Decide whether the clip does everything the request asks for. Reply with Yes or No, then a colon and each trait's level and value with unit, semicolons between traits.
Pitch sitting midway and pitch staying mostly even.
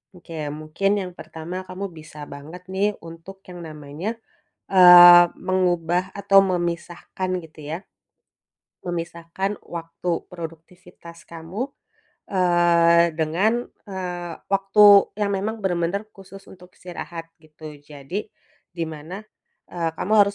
Yes: medium, 175 Hz; narrow, 2.1 semitones